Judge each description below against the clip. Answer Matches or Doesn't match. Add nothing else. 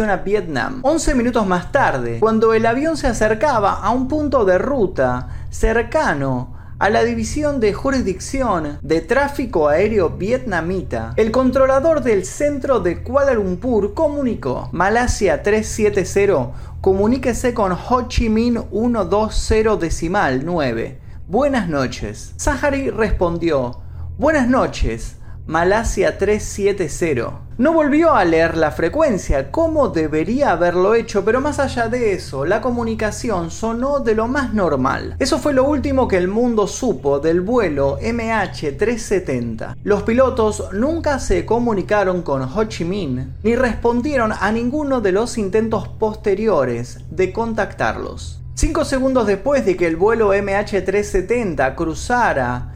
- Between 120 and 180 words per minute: Matches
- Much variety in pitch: Matches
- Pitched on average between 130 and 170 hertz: Doesn't match